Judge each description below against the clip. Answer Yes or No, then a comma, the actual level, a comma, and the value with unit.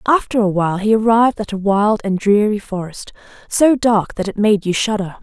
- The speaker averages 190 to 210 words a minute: Yes, fast, 205 wpm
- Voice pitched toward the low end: No, high, 210 Hz